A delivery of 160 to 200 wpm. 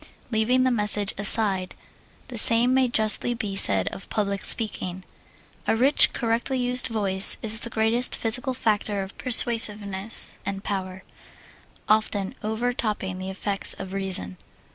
No: average, 140 wpm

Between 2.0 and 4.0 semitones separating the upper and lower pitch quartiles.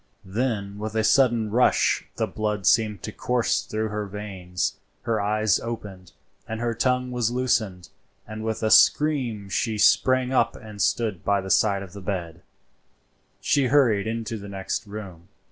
Yes: average, 2.8 semitones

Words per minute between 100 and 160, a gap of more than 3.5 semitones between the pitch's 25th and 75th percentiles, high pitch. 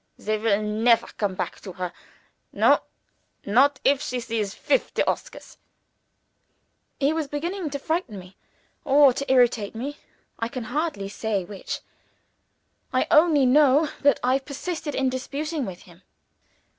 Yes: average, 140 wpm; wide, 5.4 semitones; very high, 260 Hz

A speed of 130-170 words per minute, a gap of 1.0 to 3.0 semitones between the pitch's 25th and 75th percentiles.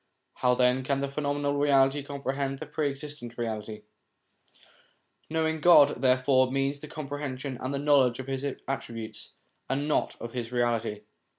Yes: average, 155 wpm; narrow, 2.4 semitones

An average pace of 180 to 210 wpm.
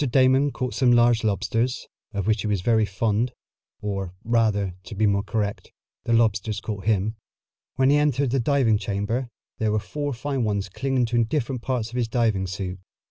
Yes: average, 185 wpm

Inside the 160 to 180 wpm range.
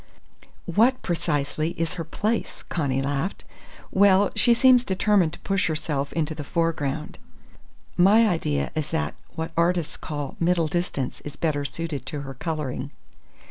No: average, 140 wpm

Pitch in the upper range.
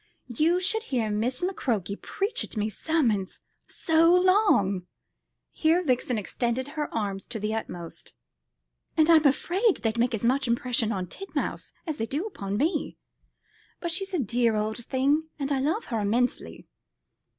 Yes: very high, 255 Hz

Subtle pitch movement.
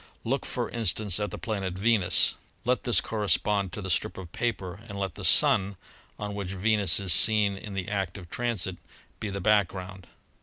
Yes: narrow, 2.2 semitones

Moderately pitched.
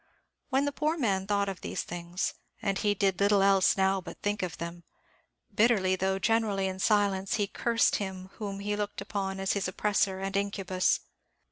No: high, 195 Hz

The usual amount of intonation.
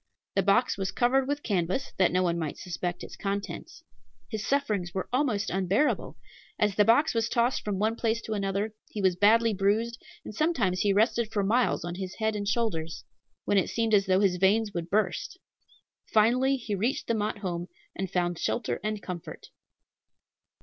Yes: average, 3.4 semitones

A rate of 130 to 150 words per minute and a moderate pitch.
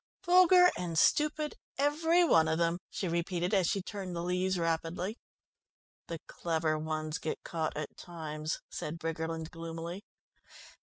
Yes: average, 140 wpm; medium, 170 Hz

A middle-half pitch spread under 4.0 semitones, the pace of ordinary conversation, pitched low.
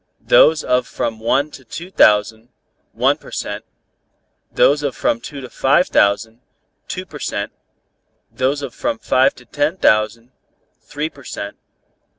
No: average, 4.3 semitones; average, 150 wpm; low, 130 Hz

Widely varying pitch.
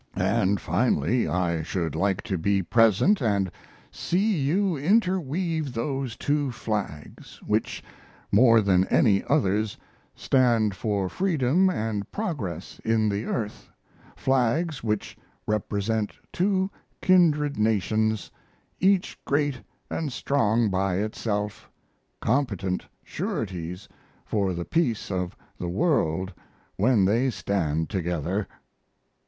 Yes: wide, 6.6 semitones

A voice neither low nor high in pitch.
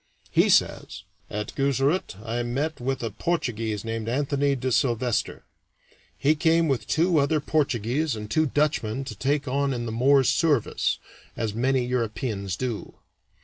No: low, 130 Hz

